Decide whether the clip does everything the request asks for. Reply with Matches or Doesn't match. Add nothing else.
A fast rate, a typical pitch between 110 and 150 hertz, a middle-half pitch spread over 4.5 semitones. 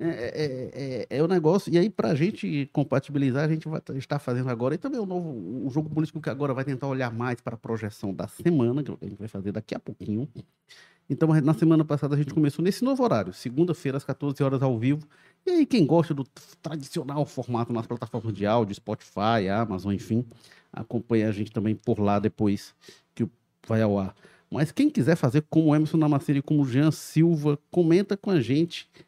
Matches